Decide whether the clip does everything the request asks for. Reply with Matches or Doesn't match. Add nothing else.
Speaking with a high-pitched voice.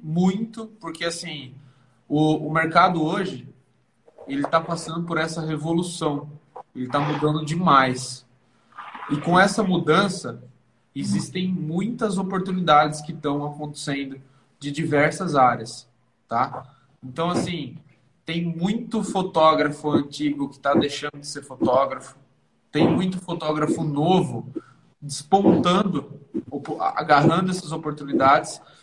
Doesn't match